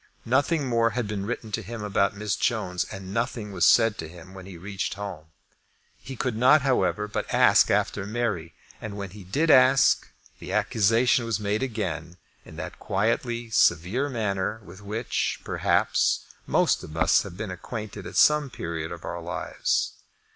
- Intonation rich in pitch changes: No, average, 4.0 semitones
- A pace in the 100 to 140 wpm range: No, average, 175 wpm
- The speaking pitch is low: Yes, low, 105 Hz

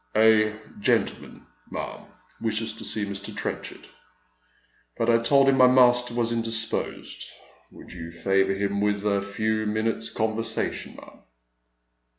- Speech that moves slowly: Yes, slow, 130 wpm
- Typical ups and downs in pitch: No, narrow, 2.1 semitones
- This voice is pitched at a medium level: No, low, 110 Hz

